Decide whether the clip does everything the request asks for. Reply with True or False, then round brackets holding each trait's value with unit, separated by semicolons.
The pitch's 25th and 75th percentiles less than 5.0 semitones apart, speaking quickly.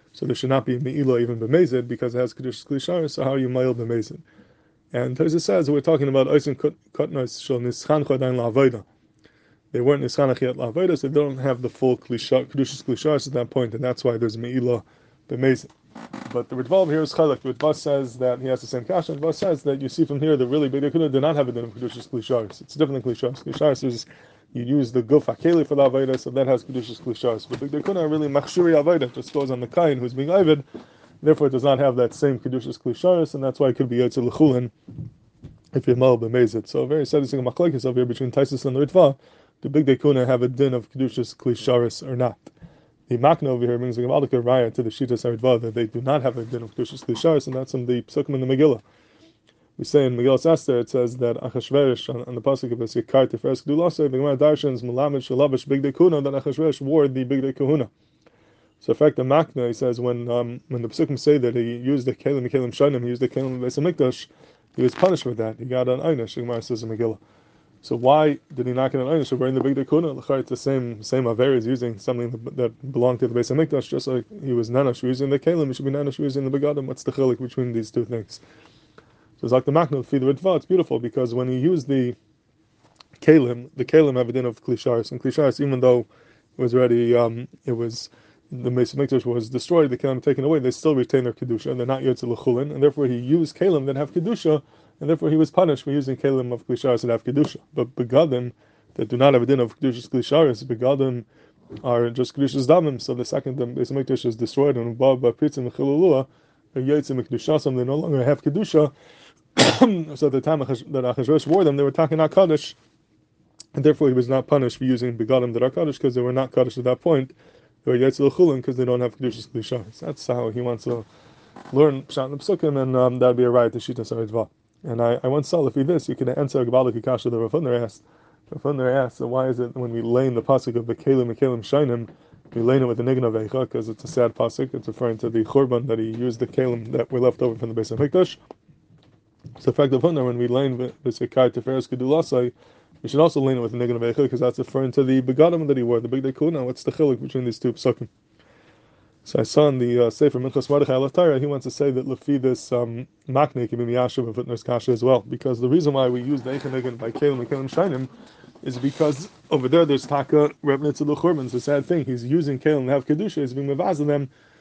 True (2.9 semitones; 230 wpm)